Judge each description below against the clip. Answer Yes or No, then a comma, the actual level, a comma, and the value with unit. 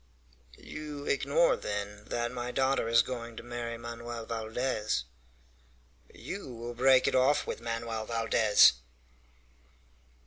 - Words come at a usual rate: No, slow, 115 wpm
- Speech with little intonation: Yes, narrow, 2.1 semitones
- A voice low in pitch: Yes, low, 120 Hz